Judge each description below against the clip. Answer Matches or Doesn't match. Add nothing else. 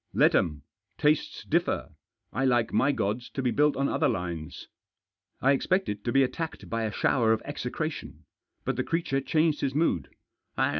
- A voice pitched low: Matches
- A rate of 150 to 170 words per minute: Doesn't match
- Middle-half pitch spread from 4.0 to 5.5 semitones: Matches